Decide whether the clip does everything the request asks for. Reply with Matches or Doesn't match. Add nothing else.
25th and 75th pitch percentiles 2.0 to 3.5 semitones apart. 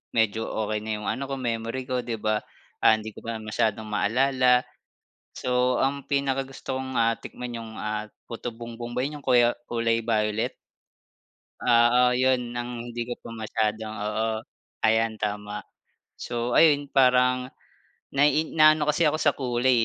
Matches